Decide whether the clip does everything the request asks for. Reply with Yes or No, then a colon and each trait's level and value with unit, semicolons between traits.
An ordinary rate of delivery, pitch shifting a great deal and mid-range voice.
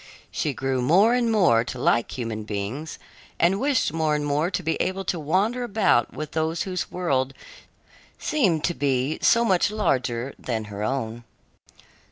Yes: average, 165 wpm; wide, 6.7 semitones; medium, 155 Hz